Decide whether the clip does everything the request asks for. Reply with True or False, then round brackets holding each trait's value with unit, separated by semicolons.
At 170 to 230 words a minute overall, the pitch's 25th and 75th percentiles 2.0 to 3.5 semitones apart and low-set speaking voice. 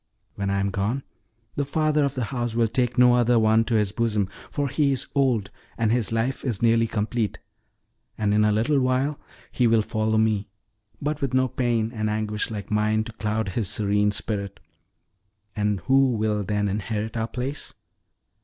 True (180 wpm; 3.0 semitones; 110 Hz)